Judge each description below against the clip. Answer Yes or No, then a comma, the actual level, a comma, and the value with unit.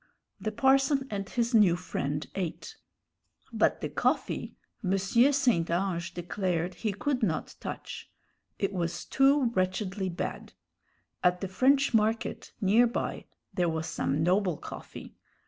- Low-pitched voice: No, high, 195 Hz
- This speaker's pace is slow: Yes, slow, 130 wpm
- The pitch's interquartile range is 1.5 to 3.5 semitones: No, average, 5.1 semitones